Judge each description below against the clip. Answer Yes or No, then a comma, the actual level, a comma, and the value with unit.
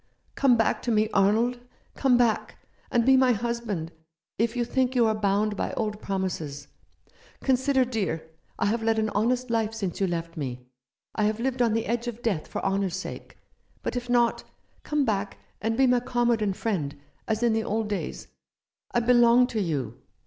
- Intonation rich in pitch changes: No, average, 3.4 semitones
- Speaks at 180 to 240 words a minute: Yes, average, 190 wpm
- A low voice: No, high, 225 Hz